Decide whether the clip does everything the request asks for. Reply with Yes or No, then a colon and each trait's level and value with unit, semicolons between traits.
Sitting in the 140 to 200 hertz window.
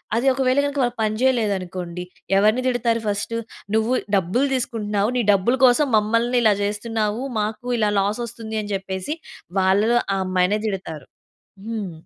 No: high, 215 Hz